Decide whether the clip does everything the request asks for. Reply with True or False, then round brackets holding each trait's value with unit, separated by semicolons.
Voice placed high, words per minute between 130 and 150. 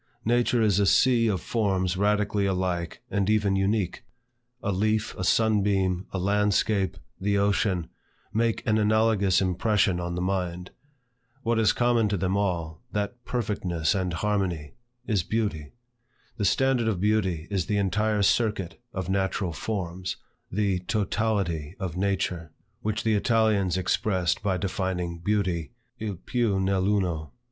False (100 Hz; 140 wpm)